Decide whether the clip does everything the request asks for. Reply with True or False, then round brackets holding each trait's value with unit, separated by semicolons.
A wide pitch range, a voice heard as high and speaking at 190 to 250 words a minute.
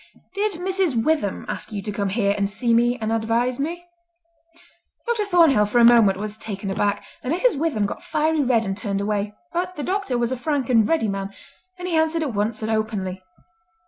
True (7.4 semitones; 235 Hz; 205 wpm)